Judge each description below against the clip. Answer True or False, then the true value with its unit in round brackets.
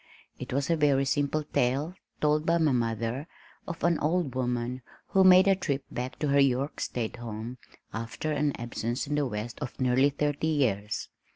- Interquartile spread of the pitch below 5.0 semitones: True (3.7 semitones)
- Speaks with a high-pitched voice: False (140 Hz)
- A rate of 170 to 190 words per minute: True (180 wpm)